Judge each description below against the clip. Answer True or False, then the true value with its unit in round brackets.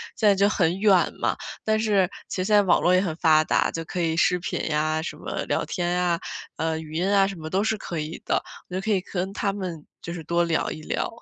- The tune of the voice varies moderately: True (3.2 semitones)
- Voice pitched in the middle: True (180 Hz)